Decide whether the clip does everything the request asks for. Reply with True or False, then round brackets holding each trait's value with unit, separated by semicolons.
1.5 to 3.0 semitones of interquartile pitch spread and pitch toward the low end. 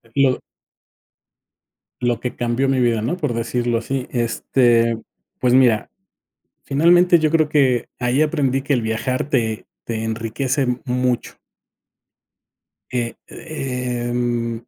True (2.5 semitones; 125 Hz)